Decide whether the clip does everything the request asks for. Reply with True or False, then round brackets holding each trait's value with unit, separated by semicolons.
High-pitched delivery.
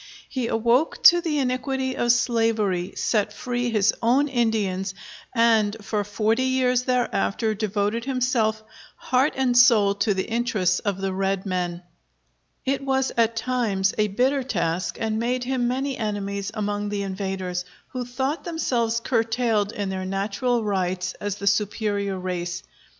True (220 Hz)